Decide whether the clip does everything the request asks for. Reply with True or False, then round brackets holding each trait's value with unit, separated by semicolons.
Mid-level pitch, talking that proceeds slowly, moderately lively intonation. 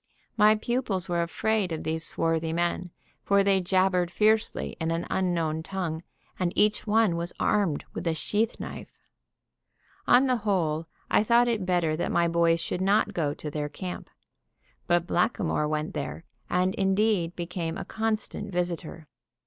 False (180 Hz; 155 wpm; 4.0 semitones)